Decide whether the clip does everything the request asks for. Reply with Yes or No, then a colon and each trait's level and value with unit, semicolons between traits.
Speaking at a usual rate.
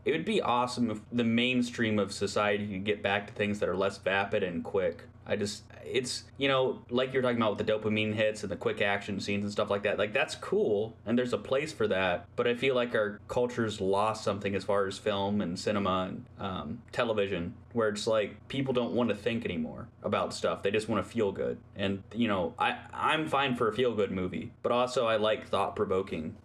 No: fast, 230 wpm